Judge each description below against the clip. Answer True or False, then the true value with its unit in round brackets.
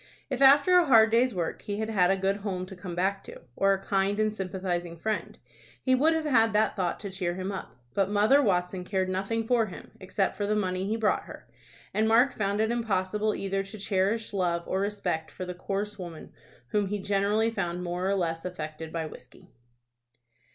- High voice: True (195 Hz)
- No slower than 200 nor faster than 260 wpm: True (205 wpm)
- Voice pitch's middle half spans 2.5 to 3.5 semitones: True (2.9 semitones)